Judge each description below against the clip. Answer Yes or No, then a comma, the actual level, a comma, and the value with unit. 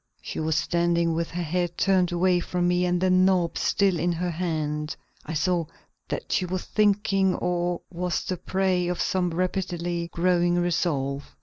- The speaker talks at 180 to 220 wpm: No, average, 170 wpm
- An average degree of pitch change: No, narrow, 1.4 semitones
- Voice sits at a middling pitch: Yes, medium, 175 Hz